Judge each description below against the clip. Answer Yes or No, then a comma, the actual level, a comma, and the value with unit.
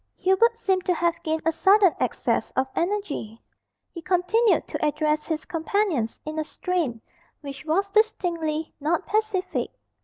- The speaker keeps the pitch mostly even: No, average, 4.3 semitones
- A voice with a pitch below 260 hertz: No, very high, 340 Hz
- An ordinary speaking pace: Yes, average, 145 wpm